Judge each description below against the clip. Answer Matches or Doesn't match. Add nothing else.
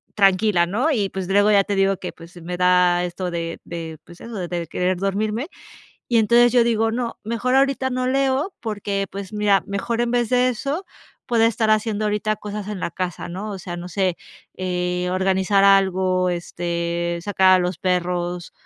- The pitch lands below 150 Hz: Doesn't match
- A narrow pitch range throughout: Doesn't match